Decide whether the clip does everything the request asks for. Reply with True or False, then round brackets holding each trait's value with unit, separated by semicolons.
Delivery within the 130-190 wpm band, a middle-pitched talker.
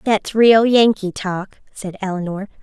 False (135 wpm; 205 Hz)